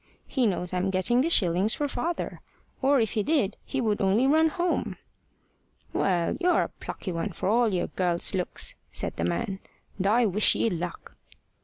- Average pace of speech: Yes, average, 180 wpm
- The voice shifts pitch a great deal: Yes, wide, 6.3 semitones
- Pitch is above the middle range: Yes, high, 210 Hz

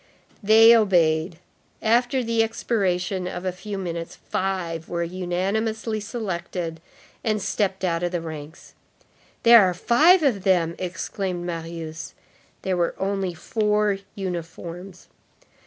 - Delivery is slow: Yes, slow, 120 wpm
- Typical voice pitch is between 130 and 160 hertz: No, medium, 185 Hz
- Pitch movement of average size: Yes, average, 3.7 semitones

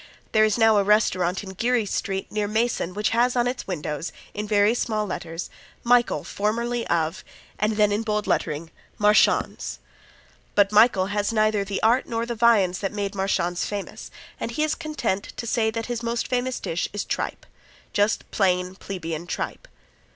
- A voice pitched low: No, high, 210 Hz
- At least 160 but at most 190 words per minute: Yes, average, 175 wpm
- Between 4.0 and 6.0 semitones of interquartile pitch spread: No, average, 3.3 semitones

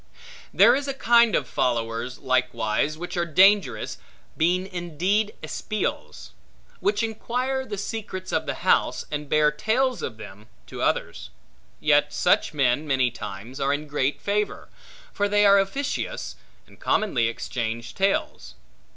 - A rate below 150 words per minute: Yes, average, 140 wpm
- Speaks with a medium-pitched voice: Yes, medium, 155 Hz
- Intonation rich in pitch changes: Yes, wide, 8.4 semitones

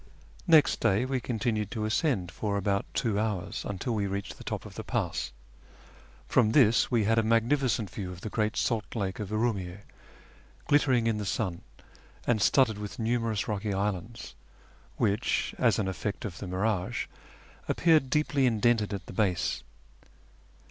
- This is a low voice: Yes, low, 110 Hz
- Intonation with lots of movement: No, average, 3.2 semitones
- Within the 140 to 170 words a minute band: Yes, average, 160 wpm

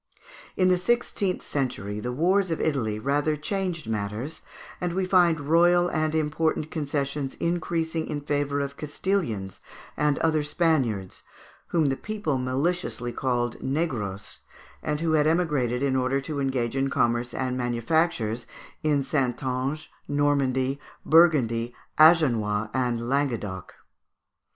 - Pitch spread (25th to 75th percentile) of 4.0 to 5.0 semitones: Yes, average, 4.6 semitones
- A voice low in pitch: No, medium, 145 Hz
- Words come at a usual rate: No, slow, 125 wpm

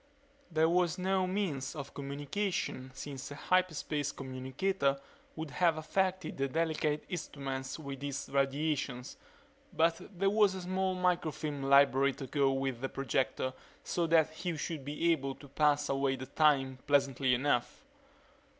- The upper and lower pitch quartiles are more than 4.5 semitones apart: No, average, 3.7 semitones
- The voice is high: No, medium, 145 Hz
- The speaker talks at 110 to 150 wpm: Yes, average, 140 wpm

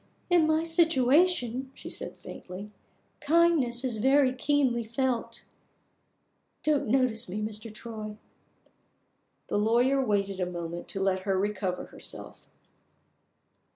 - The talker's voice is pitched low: No, high, 235 Hz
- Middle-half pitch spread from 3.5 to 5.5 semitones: Yes, average, 4.9 semitones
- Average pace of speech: No, slow, 115 wpm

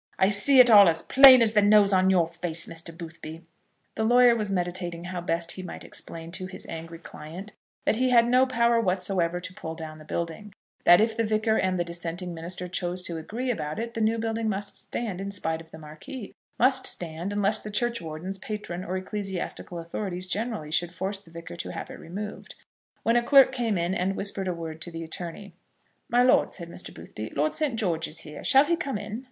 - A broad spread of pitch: No, average, 4.6 semitones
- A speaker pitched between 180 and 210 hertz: Yes, medium, 185 Hz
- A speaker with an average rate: No, fast, 215 wpm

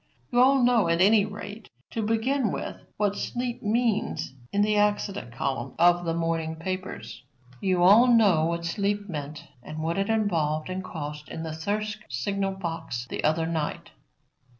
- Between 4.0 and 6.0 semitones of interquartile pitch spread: Yes, average, 4.7 semitones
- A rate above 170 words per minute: No, average, 165 wpm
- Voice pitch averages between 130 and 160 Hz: No, high, 190 Hz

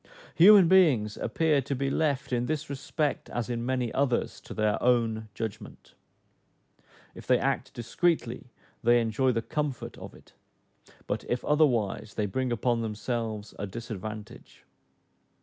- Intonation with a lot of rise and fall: No, average, 3.8 semitones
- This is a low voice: Yes, low, 120 Hz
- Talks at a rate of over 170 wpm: No, average, 140 wpm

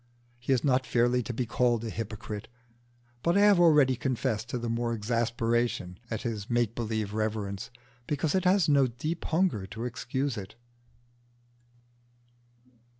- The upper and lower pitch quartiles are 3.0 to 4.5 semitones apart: Yes, average, 3.3 semitones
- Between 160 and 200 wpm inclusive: No, average, 150 wpm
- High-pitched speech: No, low, 120 Hz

